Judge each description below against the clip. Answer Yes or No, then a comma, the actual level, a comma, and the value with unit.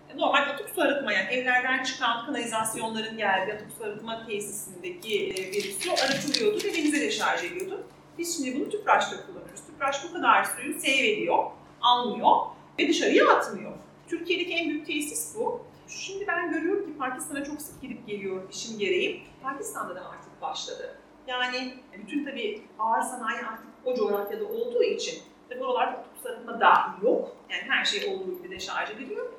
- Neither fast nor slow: No, fast, 165 wpm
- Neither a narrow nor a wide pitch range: No, wide, 8.4 semitones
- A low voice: No, very high, 315 Hz